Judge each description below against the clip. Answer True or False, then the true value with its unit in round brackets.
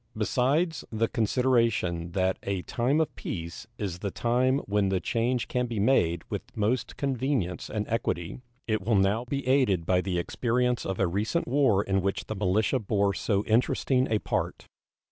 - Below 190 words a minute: True (170 wpm)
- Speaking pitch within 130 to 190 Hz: False (110 Hz)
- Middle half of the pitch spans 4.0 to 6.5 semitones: True (4.5 semitones)